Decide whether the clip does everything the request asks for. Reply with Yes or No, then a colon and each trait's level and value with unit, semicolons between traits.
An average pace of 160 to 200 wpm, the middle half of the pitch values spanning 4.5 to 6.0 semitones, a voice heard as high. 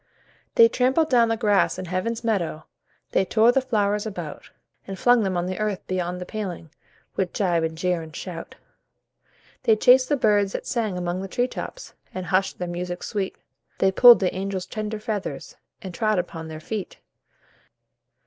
No: average, 180 wpm; average, 3.6 semitones; high, 195 Hz